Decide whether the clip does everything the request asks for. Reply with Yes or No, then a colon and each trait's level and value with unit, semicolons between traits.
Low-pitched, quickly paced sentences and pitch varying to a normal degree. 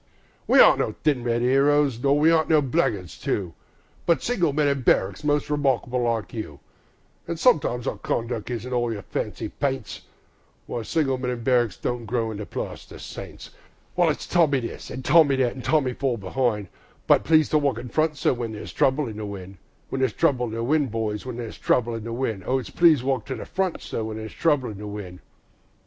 Yes: low, 125 Hz; fast, 215 wpm; average, 4.2 semitones